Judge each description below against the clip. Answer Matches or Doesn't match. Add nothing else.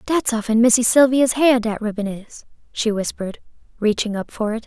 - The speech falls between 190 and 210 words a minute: Doesn't match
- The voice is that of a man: Doesn't match